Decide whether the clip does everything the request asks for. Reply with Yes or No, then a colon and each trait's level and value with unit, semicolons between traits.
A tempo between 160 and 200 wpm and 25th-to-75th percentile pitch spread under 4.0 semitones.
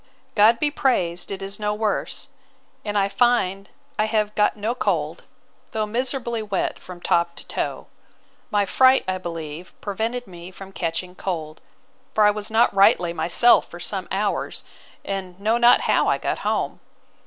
Yes: average, 165 wpm; average, 3.4 semitones